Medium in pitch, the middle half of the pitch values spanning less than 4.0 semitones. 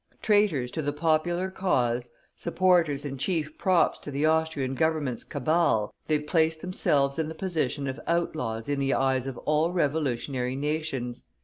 Yes: medium, 150 Hz; average, 3.5 semitones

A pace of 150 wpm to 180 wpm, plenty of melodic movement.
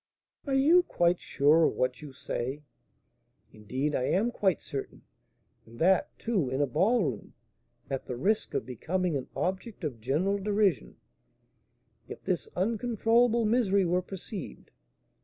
No: average, 140 wpm; wide, 7.6 semitones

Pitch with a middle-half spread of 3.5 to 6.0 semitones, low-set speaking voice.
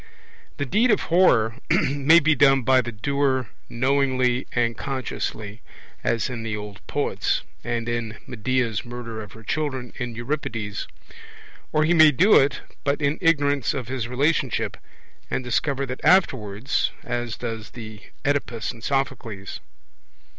Yes: average, 3.8 semitones; low, 125 Hz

